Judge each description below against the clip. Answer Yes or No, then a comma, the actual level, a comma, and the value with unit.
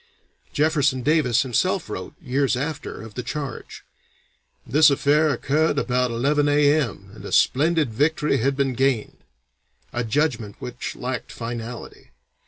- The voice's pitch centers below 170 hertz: Yes, low, 135 Hz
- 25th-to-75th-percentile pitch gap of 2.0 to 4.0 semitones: Yes, average, 3.5 semitones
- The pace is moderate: No, slow, 130 wpm